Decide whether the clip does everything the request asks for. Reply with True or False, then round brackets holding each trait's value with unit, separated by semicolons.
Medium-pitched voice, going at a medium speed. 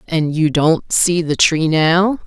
True (165 Hz; 185 wpm)